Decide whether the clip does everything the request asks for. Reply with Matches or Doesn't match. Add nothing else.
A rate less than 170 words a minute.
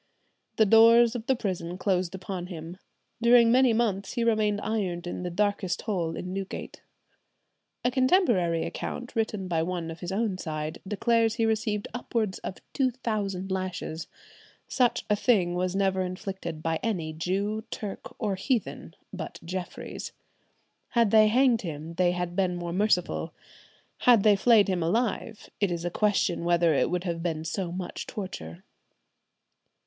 Matches